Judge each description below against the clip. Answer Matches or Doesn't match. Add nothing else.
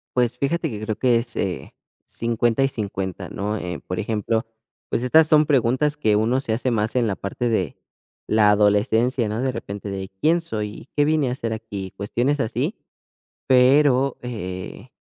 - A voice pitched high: Doesn't match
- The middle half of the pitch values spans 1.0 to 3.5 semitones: Doesn't match